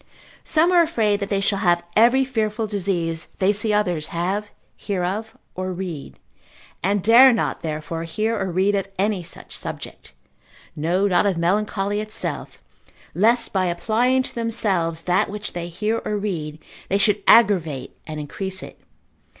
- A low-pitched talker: No, high, 200 Hz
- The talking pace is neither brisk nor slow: Yes, average, 160 wpm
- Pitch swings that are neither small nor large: Yes, average, 3.6 semitones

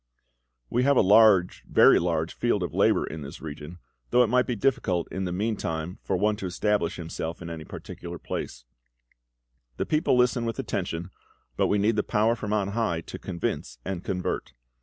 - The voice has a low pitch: Yes, very low, 95 Hz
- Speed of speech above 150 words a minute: Yes, average, 185 wpm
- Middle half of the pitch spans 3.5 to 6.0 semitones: Yes, average, 4.8 semitones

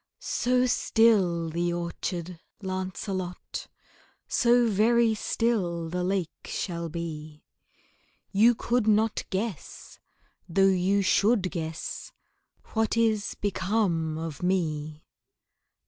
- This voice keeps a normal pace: No, slow, 95 wpm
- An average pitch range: Yes, average, 4.5 semitones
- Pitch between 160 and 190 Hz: Yes, medium, 185 Hz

